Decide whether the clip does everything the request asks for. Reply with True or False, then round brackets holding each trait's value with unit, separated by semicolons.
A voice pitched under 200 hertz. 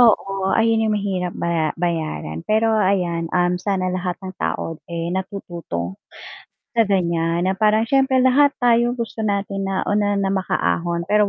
True (190 Hz)